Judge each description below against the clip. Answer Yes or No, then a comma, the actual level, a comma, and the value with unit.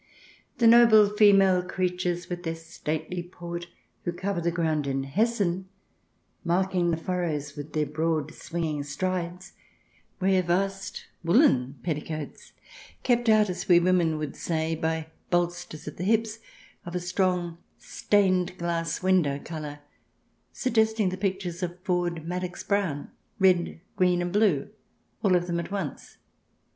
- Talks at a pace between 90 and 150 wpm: Yes, average, 140 wpm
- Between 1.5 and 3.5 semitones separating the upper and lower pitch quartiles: Yes, narrow, 2.6 semitones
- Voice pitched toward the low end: No, medium, 175 Hz